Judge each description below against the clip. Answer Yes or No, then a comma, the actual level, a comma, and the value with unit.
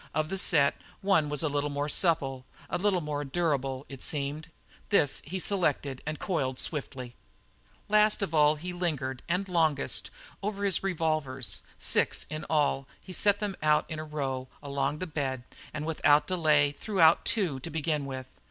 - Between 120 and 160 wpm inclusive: No, average, 170 wpm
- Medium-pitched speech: Yes, medium, 150 Hz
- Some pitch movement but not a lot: Yes, average, 4.1 semitones